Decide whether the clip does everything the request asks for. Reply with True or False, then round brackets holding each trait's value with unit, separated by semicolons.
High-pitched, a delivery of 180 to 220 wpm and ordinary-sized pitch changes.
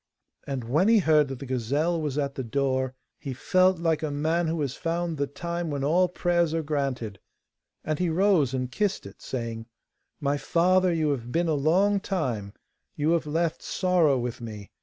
False (150 Hz; 190 wpm; 4.5 semitones)